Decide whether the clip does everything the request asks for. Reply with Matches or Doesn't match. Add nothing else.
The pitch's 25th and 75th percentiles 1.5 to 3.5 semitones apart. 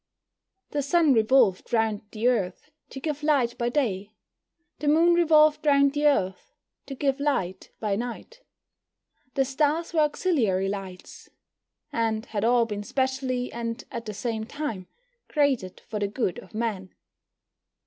Doesn't match